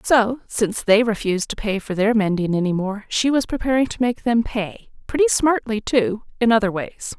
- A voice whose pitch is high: Yes, high, 220 Hz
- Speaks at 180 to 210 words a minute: Yes, average, 200 wpm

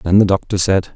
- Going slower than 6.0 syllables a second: Yes, 5.5 syllables/s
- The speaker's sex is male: Yes, male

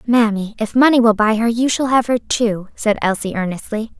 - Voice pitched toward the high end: Yes, high, 225 Hz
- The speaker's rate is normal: No, fast, 210 wpm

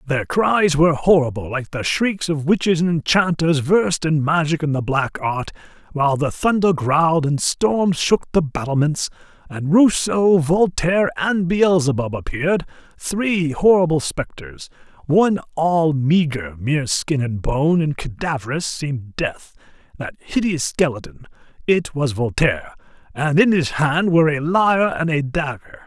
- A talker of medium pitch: Yes, medium, 155 Hz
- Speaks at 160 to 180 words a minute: No, average, 145 wpm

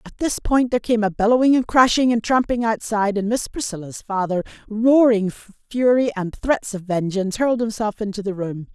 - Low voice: No, high, 220 Hz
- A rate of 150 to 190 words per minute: Yes, average, 185 wpm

